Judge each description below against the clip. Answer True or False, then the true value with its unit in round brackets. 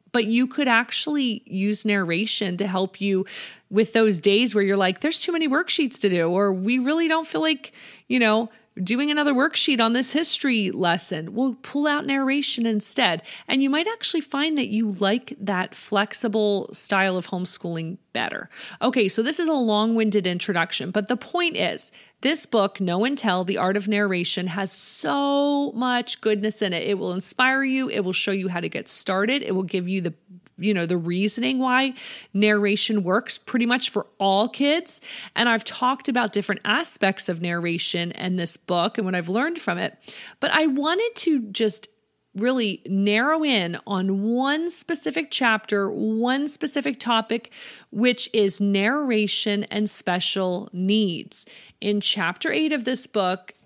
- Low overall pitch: False (215 Hz)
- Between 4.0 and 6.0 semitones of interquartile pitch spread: True (5.0 semitones)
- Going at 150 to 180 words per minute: True (170 wpm)